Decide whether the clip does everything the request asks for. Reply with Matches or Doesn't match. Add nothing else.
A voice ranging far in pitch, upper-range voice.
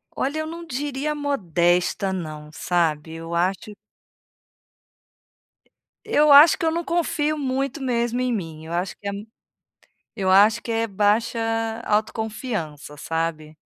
Matches